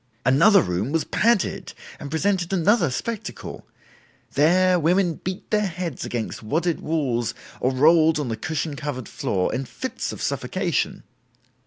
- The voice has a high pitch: No, medium, 160 Hz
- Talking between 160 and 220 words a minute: No, average, 140 wpm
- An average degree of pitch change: No, wide, 6.0 semitones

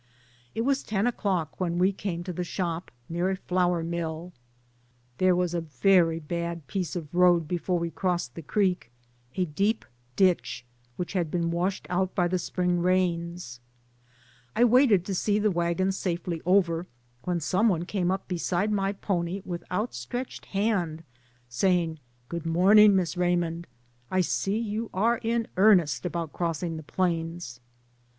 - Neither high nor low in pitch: Yes, medium, 180 Hz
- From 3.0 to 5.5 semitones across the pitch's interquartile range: No, narrow, 2.4 semitones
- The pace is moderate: Yes, average, 155 wpm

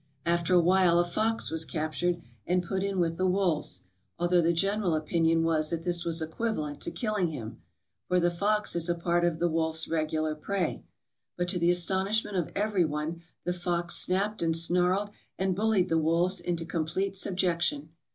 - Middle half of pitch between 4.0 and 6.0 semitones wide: No, narrow, 2.4 semitones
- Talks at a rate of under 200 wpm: Yes, average, 185 wpm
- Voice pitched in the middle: Yes, medium, 175 Hz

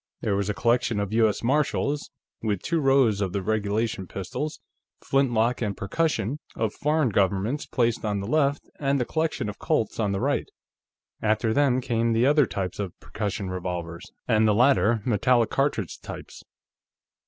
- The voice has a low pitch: Yes, low, 110 Hz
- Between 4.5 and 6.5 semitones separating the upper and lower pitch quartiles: Yes, average, 4.9 semitones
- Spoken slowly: No, average, 165 wpm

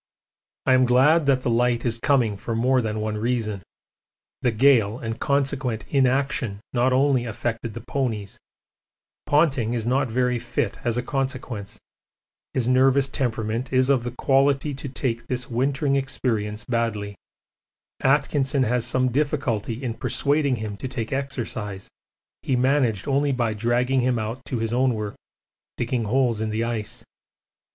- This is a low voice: Yes, low, 125 Hz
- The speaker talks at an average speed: Yes, average, 150 wpm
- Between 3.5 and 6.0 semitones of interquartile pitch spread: No, average, 3.0 semitones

